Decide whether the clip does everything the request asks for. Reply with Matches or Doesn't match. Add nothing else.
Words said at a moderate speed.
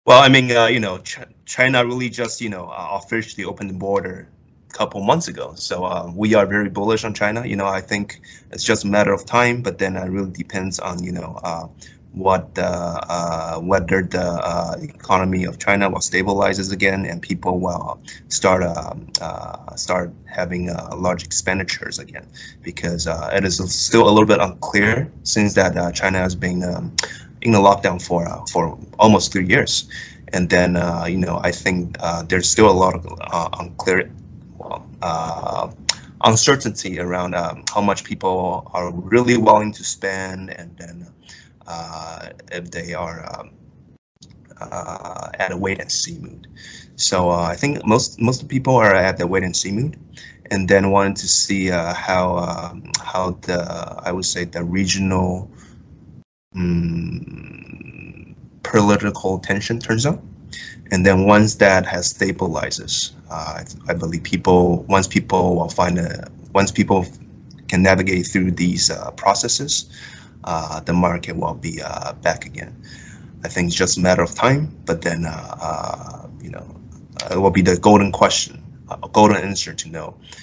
Matches